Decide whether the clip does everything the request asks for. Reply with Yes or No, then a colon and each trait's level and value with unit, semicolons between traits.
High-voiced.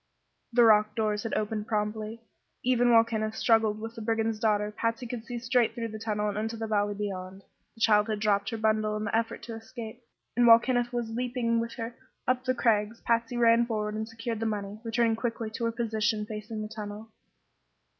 Yes: high, 225 Hz